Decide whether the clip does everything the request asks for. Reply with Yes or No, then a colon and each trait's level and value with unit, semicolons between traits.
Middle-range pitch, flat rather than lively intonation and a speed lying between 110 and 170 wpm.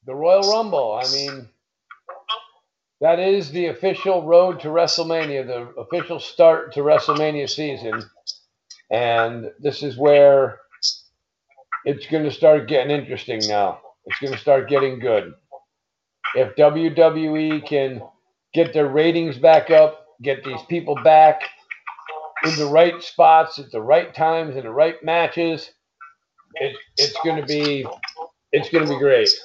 No: medium, 155 Hz; average, 3.2 semitones; average, 140 wpm